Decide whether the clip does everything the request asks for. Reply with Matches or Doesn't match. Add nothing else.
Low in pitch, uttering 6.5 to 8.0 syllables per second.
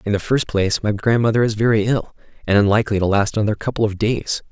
Matches